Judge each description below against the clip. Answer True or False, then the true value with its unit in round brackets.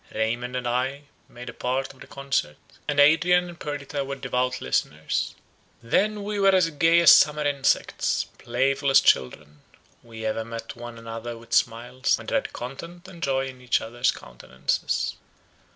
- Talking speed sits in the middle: True (165 wpm)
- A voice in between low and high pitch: False (130 Hz)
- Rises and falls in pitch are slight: False (4.1 semitones)